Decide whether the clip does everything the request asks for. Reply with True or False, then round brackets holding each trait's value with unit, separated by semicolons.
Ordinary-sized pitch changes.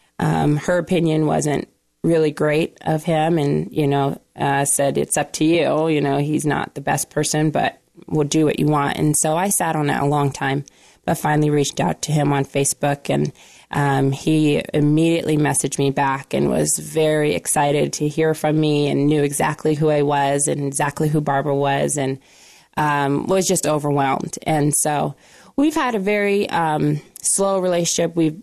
False (1.8 semitones)